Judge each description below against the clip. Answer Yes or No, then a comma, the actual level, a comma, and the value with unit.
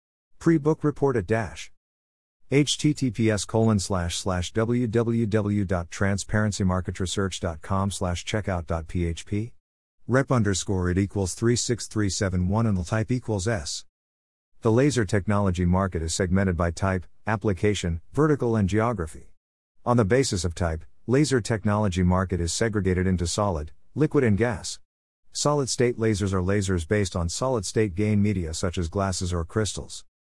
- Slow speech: Yes, slow, 125 wpm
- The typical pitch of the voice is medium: No, low, 100 Hz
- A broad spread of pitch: No, average, 4.1 semitones